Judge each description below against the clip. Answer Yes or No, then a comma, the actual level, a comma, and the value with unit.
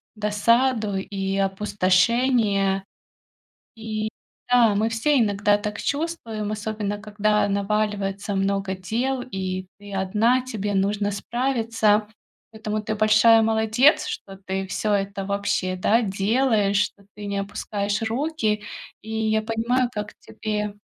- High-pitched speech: Yes, high, 210 Hz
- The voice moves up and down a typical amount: No, narrow, 2.1 semitones